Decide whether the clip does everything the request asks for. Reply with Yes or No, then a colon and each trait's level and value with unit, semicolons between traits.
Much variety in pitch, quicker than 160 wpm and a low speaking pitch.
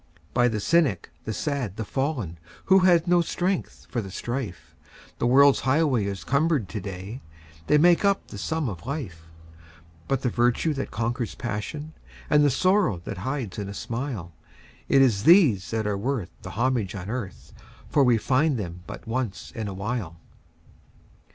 Yes: wide, 6.3 semitones; average, 170 wpm; low, 120 Hz